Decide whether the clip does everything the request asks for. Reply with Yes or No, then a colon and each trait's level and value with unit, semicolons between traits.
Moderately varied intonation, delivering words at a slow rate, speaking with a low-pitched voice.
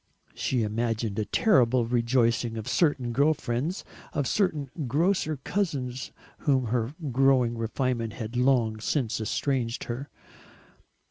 Yes: average, 3.5 semitones; slow, 125 wpm; low, 125 Hz